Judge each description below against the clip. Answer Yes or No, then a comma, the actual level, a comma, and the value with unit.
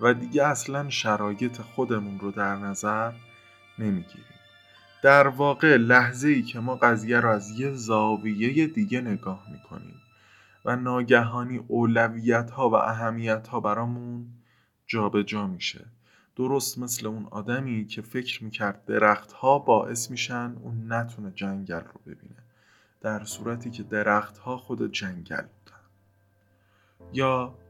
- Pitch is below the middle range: Yes, low, 115 Hz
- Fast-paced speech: No, average, 125 wpm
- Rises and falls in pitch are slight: No, average, 3.0 semitones